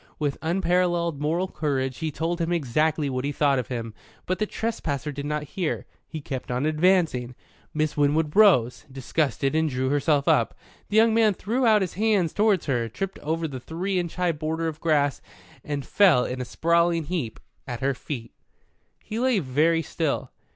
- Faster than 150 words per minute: Yes, average, 180 wpm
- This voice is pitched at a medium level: Yes, medium, 155 Hz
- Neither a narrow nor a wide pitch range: Yes, average, 4.2 semitones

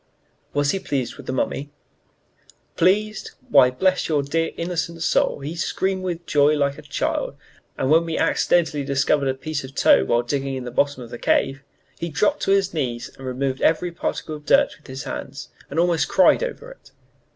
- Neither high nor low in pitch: Yes, medium, 150 Hz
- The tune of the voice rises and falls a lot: No, average, 4.1 semitones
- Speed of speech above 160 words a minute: Yes, average, 195 wpm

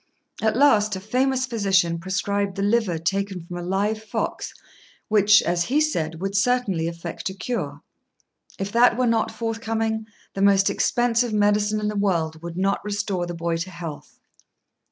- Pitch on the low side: No, high, 200 Hz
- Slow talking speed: No, average, 165 wpm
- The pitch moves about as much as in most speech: Yes, average, 3.8 semitones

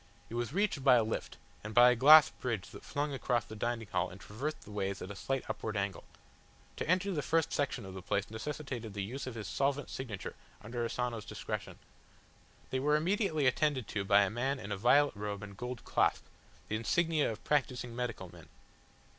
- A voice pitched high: No, low, 120 Hz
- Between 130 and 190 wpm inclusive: No, fast, 205 wpm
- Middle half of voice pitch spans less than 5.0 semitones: No, average, 5.3 semitones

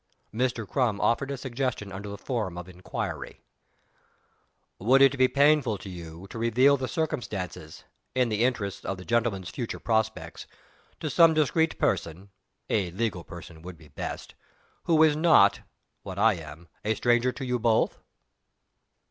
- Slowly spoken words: No, average, 155 wpm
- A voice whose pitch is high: No, low, 115 Hz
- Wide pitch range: Yes, wide, 5.7 semitones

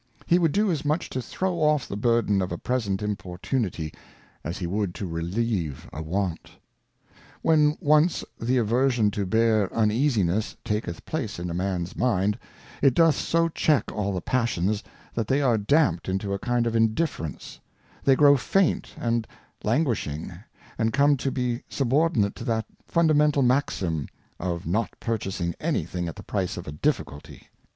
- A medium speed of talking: Yes, average, 165 wpm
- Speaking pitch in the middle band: No, low, 110 Hz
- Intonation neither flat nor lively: No, wide, 6.7 semitones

